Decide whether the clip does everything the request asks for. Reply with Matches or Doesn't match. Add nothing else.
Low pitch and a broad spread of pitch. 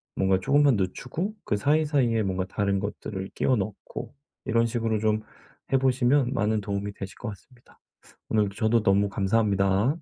Doesn't match